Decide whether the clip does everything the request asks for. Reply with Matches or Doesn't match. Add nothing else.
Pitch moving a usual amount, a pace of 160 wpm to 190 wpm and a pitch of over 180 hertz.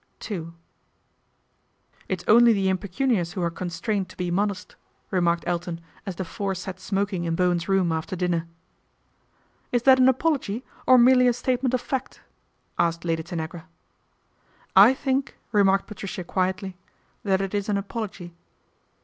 Matches